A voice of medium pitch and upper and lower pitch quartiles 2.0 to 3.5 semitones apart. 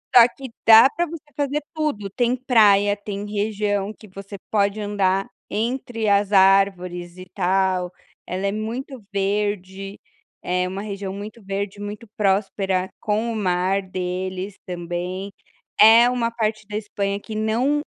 No: high, 205 Hz; narrow, 2.4 semitones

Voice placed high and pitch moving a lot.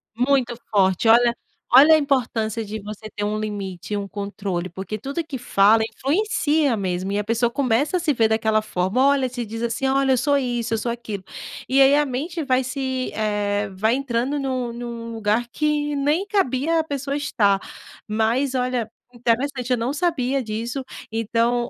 No: high, 240 Hz; average, 4.2 semitones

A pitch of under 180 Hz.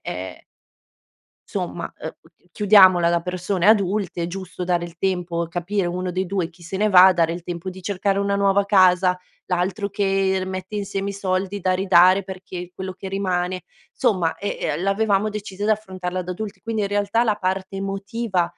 No: high, 190 Hz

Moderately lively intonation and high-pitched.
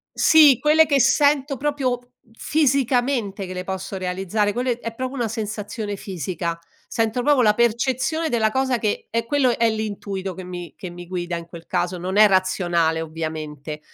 No: wide, 5.8 semitones; high, 215 Hz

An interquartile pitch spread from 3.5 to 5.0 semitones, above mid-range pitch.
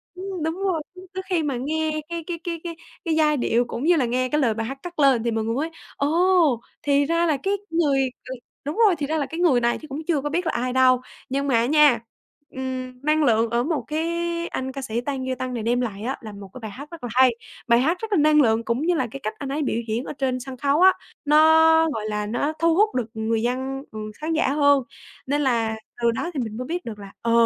Yes: average, 4.6 semitones; very high, 275 Hz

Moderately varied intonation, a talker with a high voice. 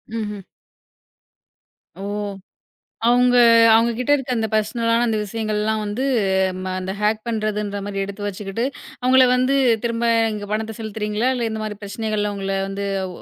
No: narrow, 2.1 semitones; high, 215 Hz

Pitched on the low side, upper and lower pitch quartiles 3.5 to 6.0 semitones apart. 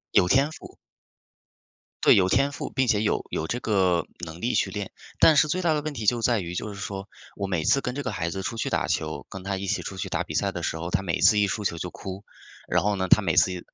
Yes: low, 100 Hz; average, 4.9 semitones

